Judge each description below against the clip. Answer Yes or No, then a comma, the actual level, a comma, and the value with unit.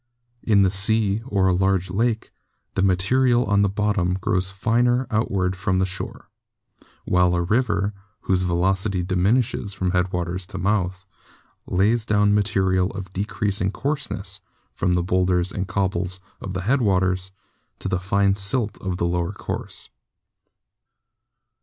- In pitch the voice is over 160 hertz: No, very low, 95 Hz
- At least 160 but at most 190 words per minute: No, average, 140 wpm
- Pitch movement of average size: No, narrow, 2.0 semitones